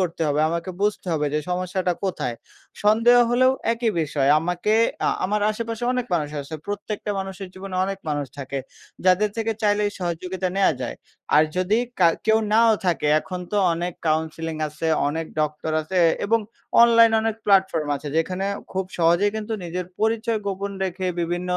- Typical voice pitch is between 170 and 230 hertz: Yes, medium, 185 Hz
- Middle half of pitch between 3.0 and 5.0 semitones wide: Yes, average, 4.2 semitones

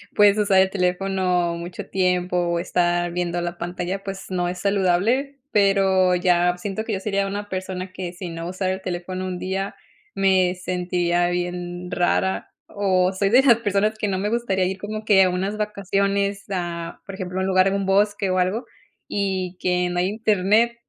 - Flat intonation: Yes, narrow, 1.8 semitones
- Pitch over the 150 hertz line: Yes, high, 190 Hz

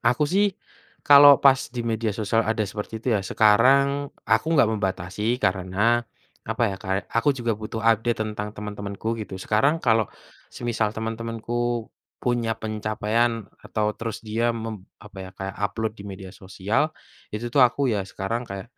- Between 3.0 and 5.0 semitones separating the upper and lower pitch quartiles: No, narrow, 2.4 semitones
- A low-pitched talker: Yes, low, 110 Hz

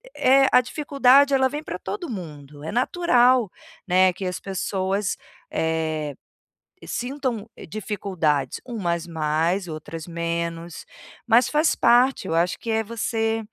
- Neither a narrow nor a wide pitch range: No, wide, 6.8 semitones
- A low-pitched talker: No, high, 200 Hz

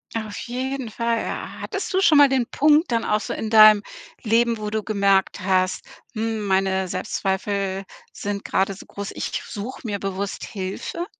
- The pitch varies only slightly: No, average, 3.2 semitones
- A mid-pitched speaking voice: No, high, 210 Hz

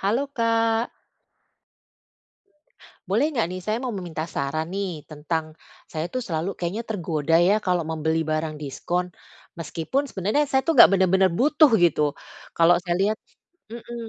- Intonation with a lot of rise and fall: Yes, wide, 5.9 semitones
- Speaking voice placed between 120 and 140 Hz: No, medium, 185 Hz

